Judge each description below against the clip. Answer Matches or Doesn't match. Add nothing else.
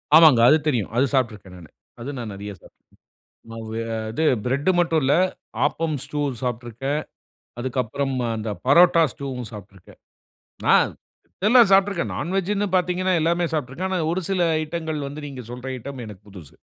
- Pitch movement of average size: Doesn't match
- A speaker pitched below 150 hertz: Matches